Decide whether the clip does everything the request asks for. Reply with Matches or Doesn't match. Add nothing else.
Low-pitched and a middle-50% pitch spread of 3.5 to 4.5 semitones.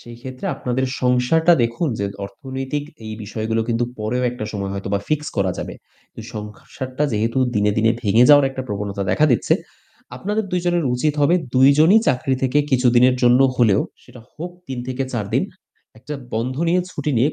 Matches